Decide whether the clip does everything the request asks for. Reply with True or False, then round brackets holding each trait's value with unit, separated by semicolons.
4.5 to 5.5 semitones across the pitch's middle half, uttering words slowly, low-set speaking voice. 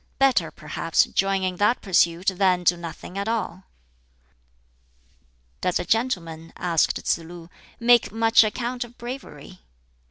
False (5.1 semitones; 130 wpm; 190 Hz)